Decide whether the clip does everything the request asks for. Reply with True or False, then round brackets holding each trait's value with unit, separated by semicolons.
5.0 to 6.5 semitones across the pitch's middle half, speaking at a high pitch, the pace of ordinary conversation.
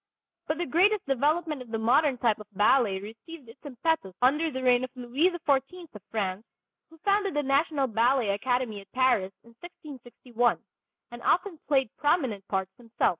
True (5.3 semitones; 255 Hz; 170 wpm)